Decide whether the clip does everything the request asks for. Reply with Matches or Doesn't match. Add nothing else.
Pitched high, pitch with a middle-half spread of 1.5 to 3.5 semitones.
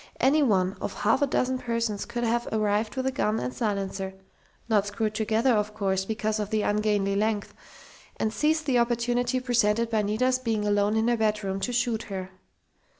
Matches